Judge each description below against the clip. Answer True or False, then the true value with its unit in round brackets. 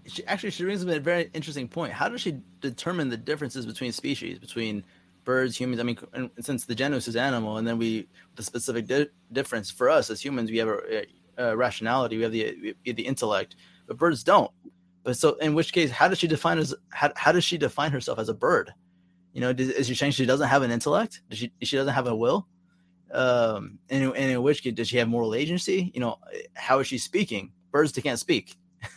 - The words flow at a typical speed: False (230 wpm)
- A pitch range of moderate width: True (4.7 semitones)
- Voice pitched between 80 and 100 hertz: False (130 Hz)